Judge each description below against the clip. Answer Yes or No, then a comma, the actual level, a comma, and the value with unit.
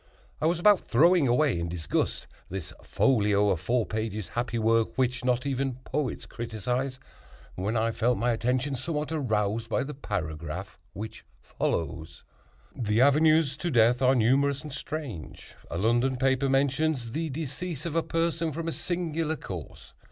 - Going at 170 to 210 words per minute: No, average, 155 wpm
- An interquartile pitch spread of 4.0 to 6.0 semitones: Yes, average, 5.3 semitones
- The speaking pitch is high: No, low, 125 Hz